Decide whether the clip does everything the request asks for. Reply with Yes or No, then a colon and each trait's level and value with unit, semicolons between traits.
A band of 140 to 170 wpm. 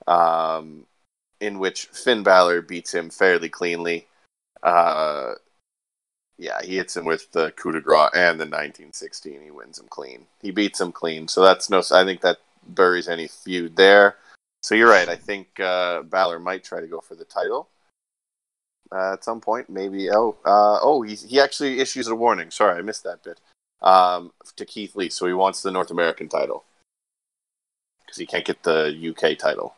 No: average, 185 wpm